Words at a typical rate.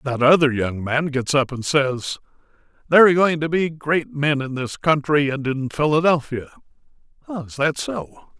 Yes: average, 170 wpm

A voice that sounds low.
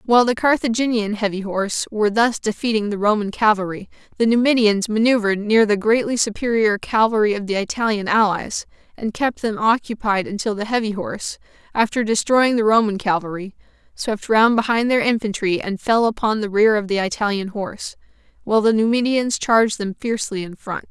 No: high, 215 Hz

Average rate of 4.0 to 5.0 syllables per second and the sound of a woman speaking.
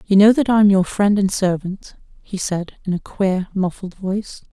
Yes: 4.7 syllables/s; female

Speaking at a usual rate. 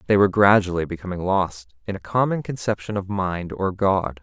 Yes: average, 185 wpm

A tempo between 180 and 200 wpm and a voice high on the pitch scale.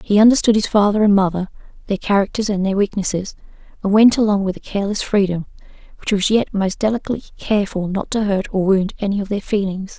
Yes: average, 190 wpm; high, 200 Hz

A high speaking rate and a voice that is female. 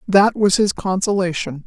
No: average, 145 wpm; female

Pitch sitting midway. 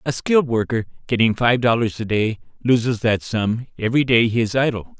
No: low, 115 Hz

